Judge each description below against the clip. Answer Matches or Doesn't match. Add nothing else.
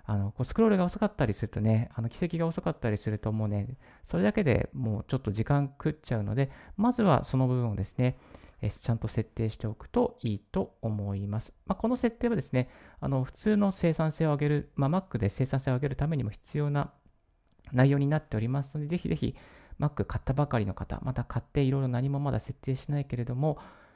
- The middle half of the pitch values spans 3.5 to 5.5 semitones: Matches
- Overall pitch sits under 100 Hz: Doesn't match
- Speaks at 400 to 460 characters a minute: Matches